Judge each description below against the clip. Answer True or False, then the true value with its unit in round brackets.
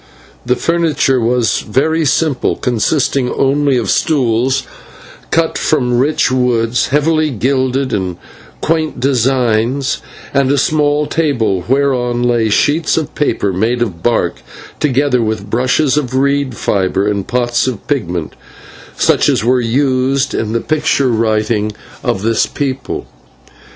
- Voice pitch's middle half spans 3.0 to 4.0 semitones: True (3.7 semitones)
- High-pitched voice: False (130 Hz)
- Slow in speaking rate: True (130 wpm)